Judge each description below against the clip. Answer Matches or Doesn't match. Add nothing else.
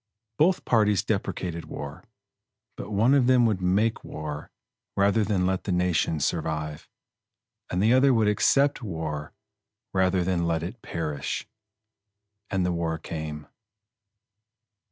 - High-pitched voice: Doesn't match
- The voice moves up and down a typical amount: Matches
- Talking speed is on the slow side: Matches